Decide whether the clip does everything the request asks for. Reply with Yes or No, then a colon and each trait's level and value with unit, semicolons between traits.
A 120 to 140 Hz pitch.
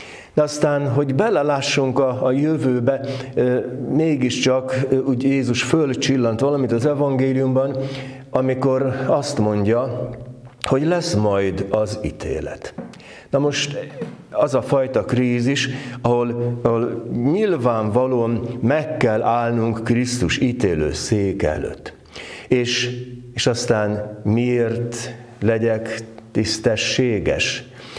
Yes: low, 125 Hz